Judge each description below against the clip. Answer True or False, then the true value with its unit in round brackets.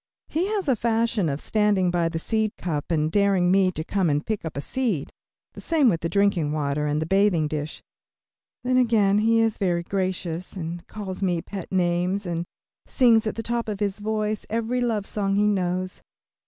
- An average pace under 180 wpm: False (195 wpm)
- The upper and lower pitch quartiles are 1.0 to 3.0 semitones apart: False (4.1 semitones)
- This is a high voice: True (195 Hz)